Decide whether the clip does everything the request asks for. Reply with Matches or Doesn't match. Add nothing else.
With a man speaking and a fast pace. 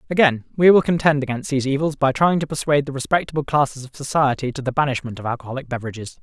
Matches